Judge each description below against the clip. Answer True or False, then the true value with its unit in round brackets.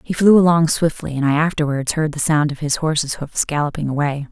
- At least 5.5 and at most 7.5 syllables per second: True (5.7 syllables/s)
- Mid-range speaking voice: True (150 Hz)